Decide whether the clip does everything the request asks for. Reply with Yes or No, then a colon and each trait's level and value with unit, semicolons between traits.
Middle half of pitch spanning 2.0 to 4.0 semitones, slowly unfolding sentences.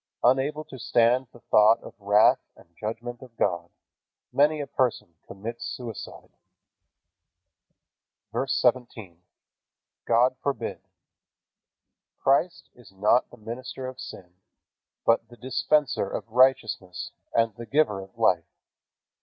Yes: average, 3.6 semitones; slow, 120 wpm